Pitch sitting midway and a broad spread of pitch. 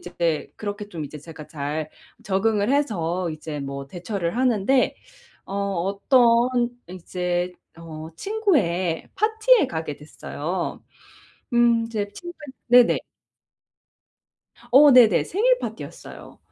No: high, 195 Hz; wide, 6.8 semitones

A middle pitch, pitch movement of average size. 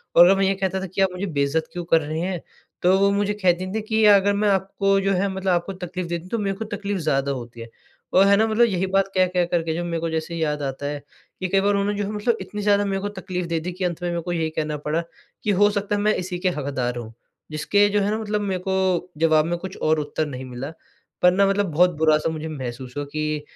Yes: medium, 180 Hz; average, 3.9 semitones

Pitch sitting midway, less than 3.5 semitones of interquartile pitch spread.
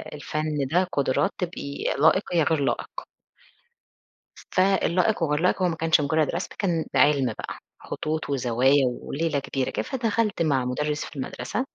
No: medium, 155 Hz; average, 3.8 semitones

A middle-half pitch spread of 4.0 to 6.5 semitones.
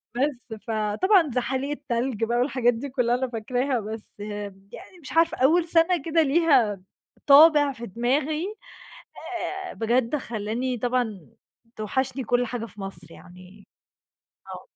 Yes: average, 4.6 semitones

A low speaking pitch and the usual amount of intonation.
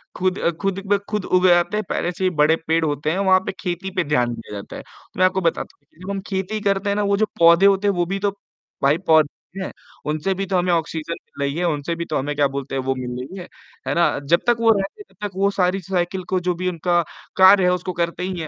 No: medium, 180 Hz; average, 3.3 semitones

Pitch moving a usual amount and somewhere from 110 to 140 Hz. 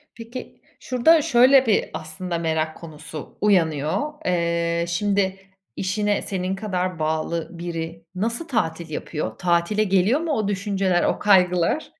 No: average, 4.1 semitones; medium, 185 Hz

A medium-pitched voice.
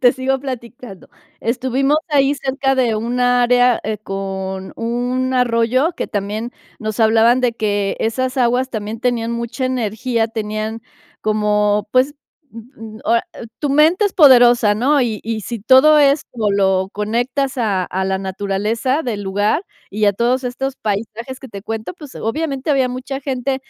No: high, 235 Hz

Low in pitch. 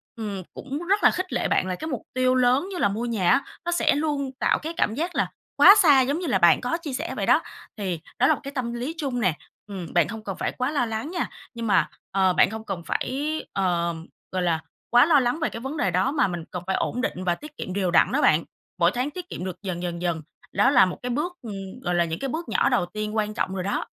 No: high, 235 Hz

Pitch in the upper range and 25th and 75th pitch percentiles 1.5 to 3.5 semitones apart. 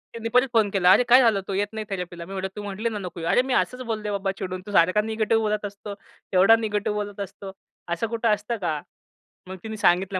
Yes: high, 205 Hz; narrow, 2.5 semitones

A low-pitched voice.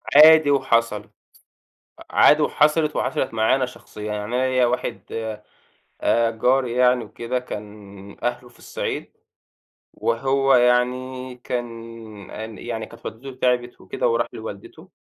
Yes: low, 125 Hz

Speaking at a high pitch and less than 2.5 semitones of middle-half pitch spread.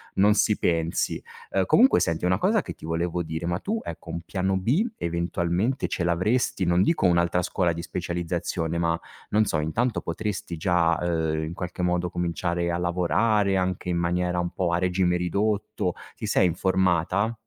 No: very low, 90 Hz; narrow, 1.8 semitones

